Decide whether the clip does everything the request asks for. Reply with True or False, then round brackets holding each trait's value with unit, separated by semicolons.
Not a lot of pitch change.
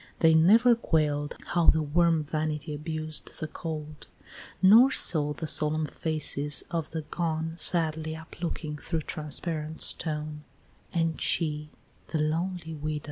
True (1.5 semitones)